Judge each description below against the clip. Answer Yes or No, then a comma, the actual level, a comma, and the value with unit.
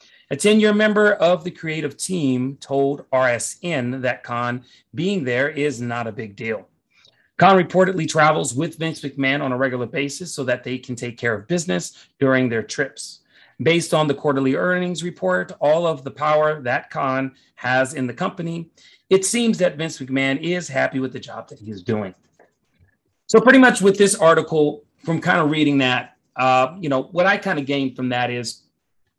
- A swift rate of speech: No, average, 190 wpm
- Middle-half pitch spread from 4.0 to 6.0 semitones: Yes, average, 5.2 semitones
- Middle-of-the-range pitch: Yes, medium, 145 Hz